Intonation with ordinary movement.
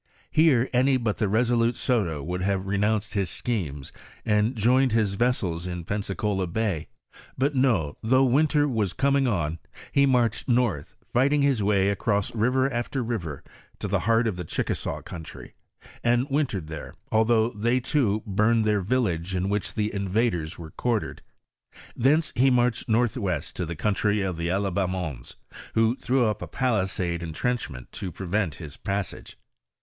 Yes: average, 4.9 semitones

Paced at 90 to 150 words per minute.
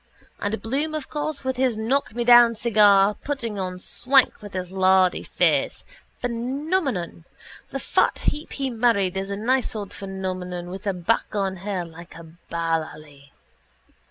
Yes: average, 145 wpm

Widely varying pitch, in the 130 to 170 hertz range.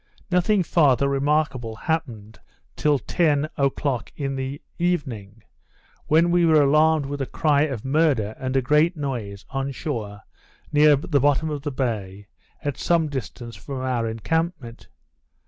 No: average, 4.1 semitones; medium, 140 Hz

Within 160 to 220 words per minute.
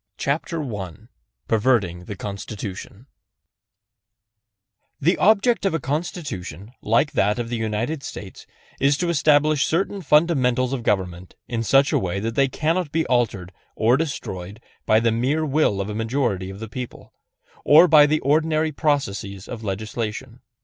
No: average, 150 wpm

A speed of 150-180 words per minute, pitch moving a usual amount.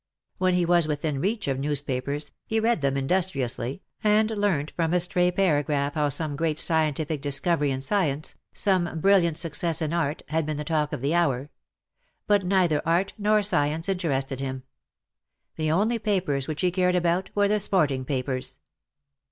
Yes: average, 170 wpm; average, 4.4 semitones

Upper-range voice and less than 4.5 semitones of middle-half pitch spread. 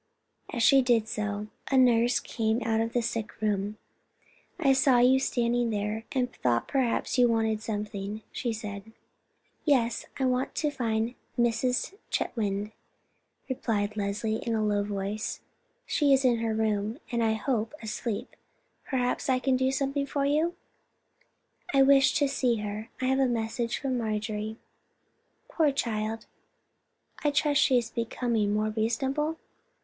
Yes: high, 230 Hz; average, 3.4 semitones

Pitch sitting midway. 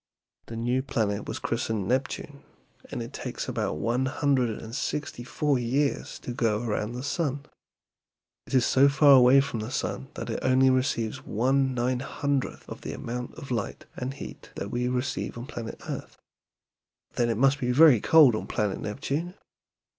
No: low, 125 Hz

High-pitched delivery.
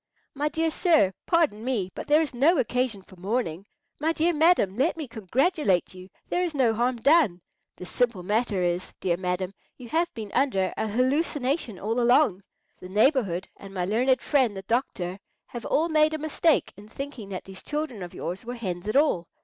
Yes: high, 240 Hz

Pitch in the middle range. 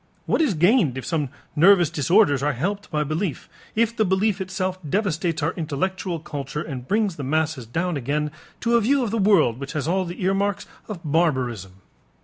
Yes: medium, 170 Hz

